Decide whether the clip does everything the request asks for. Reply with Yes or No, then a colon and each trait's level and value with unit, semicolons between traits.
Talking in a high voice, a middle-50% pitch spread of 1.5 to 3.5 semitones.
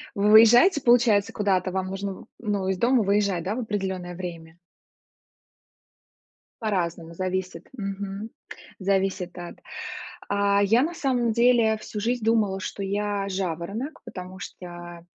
Yes: high, 200 Hz; average, 2.9 semitones